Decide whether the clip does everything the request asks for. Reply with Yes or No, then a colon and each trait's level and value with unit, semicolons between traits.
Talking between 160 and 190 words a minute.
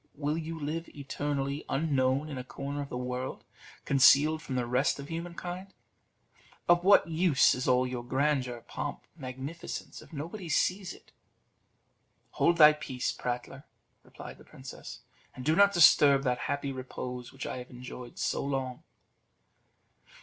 No: average, 150 wpm